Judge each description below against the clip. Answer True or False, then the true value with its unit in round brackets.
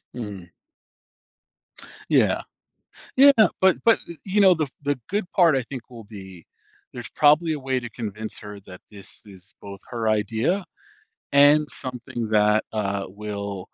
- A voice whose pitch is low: True (115 Hz)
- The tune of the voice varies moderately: False (6.3 semitones)